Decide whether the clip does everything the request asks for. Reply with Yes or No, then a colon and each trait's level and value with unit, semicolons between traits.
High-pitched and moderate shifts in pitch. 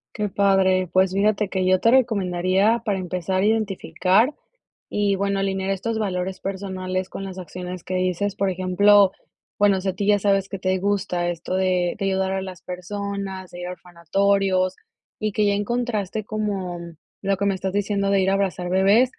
No: high, 195 Hz; narrow, 1.5 semitones